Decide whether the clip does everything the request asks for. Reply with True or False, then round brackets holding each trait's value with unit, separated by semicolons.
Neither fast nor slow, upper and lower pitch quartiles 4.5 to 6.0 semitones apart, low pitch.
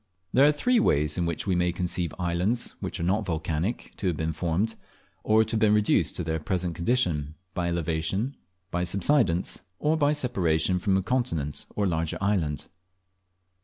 True (175 wpm; 5.0 semitones; 90 Hz)